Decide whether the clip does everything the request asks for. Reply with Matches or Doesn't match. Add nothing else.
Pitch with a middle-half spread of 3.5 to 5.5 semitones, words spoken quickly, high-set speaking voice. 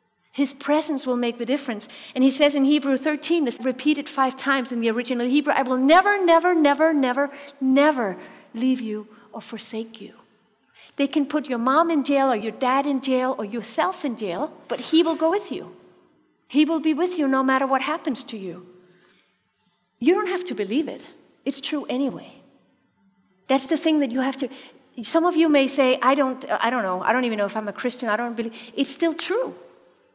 Matches